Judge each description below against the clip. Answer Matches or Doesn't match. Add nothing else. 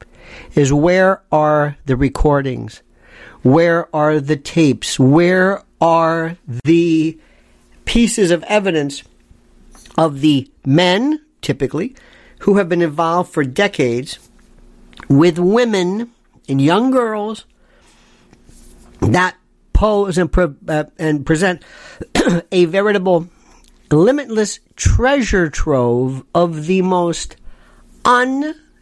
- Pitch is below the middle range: Doesn't match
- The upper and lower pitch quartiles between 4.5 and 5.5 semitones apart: Matches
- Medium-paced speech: Doesn't match